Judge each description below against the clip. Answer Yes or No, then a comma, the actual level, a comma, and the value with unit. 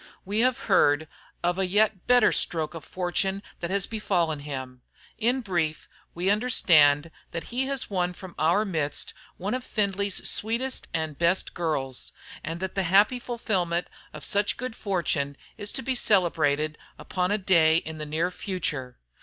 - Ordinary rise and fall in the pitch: Yes, average, 4.7 semitones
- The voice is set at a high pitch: No, medium, 180 Hz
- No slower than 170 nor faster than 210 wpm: No, average, 160 wpm